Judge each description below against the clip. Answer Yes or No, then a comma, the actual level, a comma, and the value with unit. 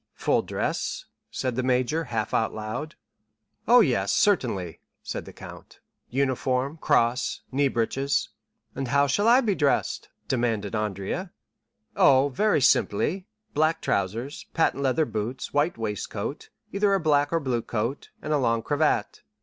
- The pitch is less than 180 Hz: Yes, low, 135 Hz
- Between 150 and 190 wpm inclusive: No, average, 140 wpm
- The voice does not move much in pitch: No, average, 5.0 semitones